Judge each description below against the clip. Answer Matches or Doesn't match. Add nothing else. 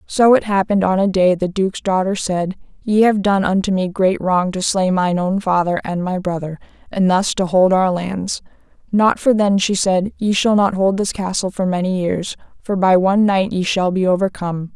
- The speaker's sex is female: Matches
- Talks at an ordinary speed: Doesn't match